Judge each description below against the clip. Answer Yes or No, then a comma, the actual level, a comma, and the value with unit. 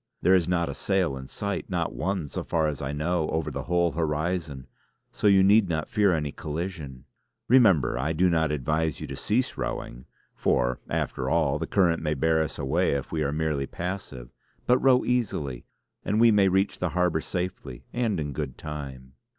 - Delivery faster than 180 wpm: Yes, average, 190 wpm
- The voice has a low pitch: Yes, very low, 80 Hz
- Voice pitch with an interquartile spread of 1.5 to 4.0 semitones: No, average, 4.5 semitones